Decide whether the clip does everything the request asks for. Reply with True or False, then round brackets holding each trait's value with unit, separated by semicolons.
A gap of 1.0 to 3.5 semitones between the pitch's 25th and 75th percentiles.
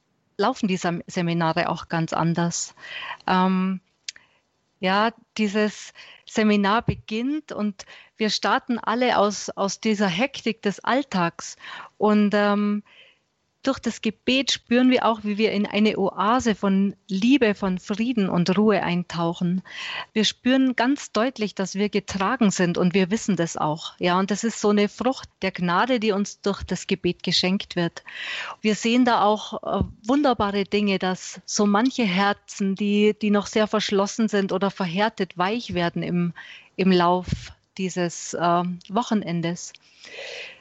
True (3.2 semitones)